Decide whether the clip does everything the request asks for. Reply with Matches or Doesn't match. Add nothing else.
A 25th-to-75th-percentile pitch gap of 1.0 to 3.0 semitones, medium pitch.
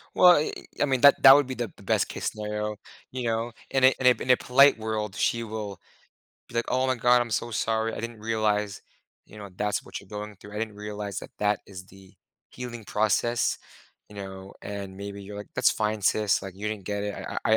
Doesn't match